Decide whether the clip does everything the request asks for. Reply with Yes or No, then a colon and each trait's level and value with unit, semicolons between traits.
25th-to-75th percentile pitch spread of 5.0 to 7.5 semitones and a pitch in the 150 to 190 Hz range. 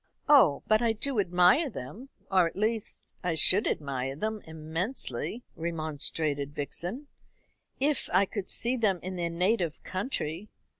Yes: wide, 5.6 semitones; medium, 185 Hz